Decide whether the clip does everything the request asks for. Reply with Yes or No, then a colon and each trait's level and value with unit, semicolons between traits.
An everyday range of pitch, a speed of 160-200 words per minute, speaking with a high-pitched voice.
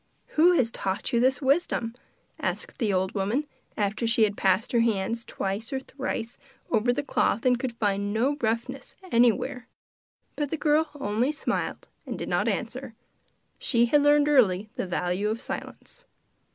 Yes: average, 4.2 semitones; average, 165 wpm; high, 235 Hz